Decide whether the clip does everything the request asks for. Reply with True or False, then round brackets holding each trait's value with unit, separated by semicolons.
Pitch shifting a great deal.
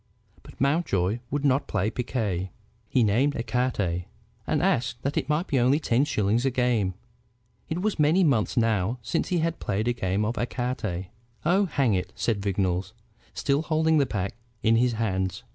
True (5.8 semitones)